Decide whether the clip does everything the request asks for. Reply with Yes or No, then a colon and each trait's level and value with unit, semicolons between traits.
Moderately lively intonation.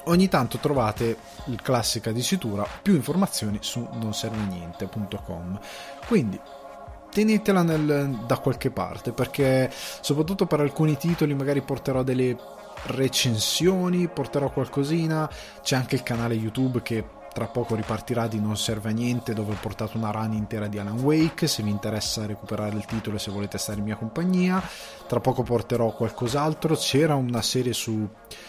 Yes: average, 4.7 semitones